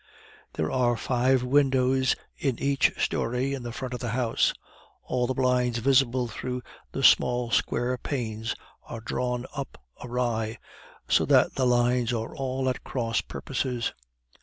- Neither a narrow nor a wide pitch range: No, narrow, 1.5 semitones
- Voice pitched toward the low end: Yes, low, 125 Hz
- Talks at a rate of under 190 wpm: Yes, average, 145 wpm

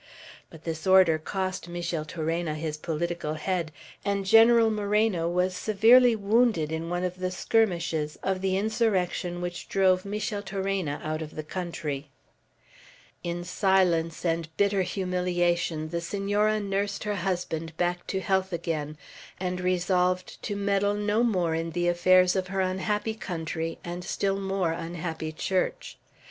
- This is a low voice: No, medium, 180 Hz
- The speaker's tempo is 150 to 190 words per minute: No, average, 140 wpm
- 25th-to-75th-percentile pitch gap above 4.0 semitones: No, average, 3.0 semitones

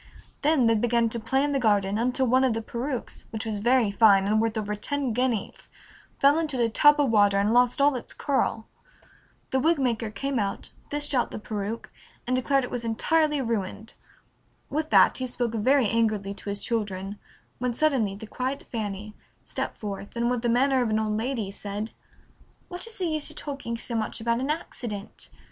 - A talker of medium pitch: No, high, 235 Hz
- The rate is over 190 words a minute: Yes, average, 200 wpm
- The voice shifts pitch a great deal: No, average, 3.8 semitones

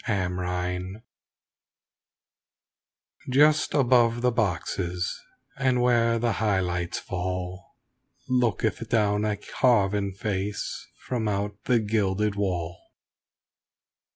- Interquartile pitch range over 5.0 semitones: No, average, 4.0 semitones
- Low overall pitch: Yes, low, 105 Hz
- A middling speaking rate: No, slow, 95 wpm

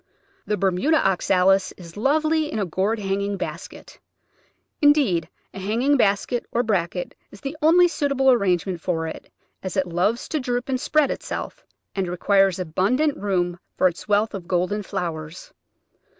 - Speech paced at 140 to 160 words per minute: Yes, average, 155 wpm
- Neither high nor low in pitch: No, high, 200 Hz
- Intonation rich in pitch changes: Yes, wide, 5.9 semitones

